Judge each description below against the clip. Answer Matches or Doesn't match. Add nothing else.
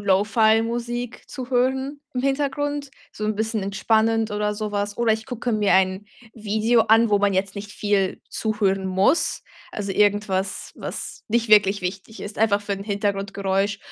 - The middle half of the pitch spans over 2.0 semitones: Matches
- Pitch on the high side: Matches